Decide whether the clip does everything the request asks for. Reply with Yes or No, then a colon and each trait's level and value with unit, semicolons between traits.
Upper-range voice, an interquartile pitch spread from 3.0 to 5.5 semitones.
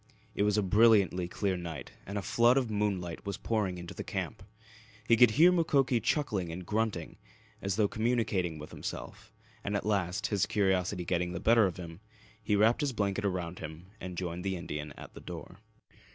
No: low, 100 Hz; average, 3.6 semitones